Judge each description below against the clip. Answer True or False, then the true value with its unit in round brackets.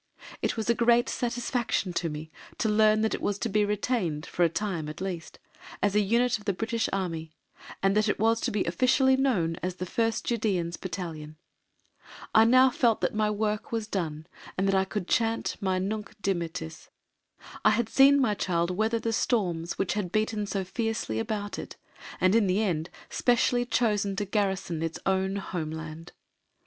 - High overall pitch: True (205 Hz)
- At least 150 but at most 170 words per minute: False (185 wpm)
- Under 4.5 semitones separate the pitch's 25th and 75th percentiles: True (4.1 semitones)